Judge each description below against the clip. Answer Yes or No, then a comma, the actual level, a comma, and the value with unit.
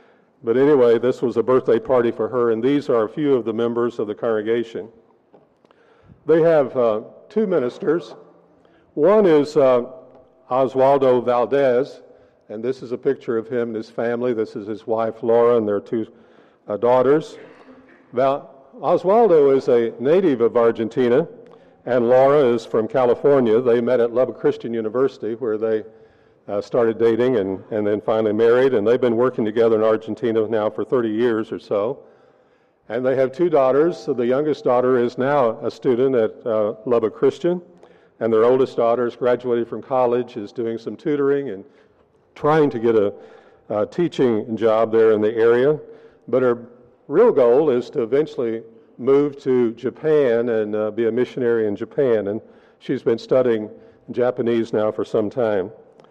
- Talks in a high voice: No, low, 125 Hz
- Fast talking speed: No, average, 170 wpm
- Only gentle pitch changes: No, average, 3.6 semitones